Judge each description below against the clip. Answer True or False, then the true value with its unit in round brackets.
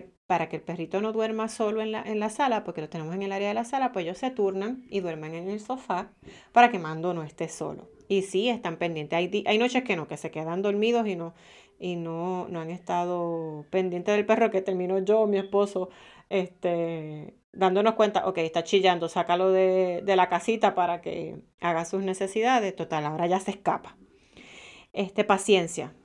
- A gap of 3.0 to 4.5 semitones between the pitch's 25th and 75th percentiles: True (3.4 semitones)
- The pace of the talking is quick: True (205 wpm)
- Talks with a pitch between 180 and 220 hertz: True (185 Hz)